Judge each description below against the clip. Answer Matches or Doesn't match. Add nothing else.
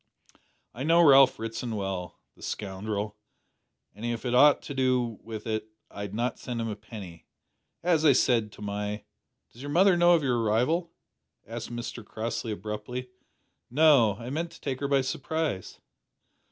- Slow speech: Doesn't match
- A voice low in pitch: Matches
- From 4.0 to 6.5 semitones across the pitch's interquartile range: Matches